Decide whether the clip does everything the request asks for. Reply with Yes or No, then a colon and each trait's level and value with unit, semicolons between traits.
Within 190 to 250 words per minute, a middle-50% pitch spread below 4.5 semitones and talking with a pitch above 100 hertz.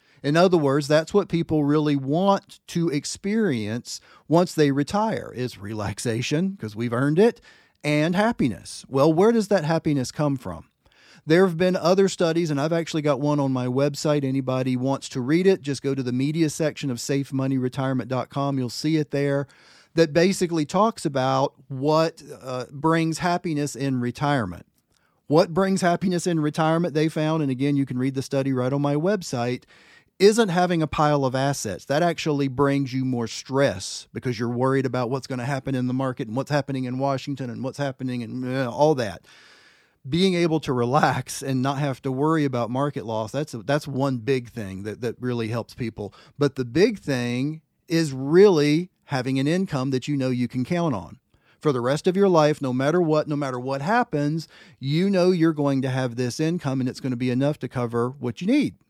Yes: average, 195 wpm; average, 3.9 semitones; medium, 140 Hz